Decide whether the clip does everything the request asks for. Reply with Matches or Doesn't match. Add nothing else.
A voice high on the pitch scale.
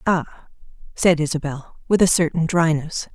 Doesn't match